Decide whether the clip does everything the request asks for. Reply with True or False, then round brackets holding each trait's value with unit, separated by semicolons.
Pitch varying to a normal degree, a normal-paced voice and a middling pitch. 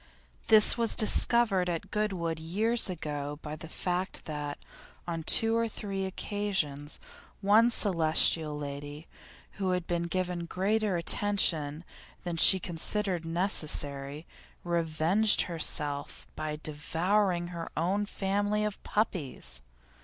False (4.7 semitones; 115 wpm; 175 Hz)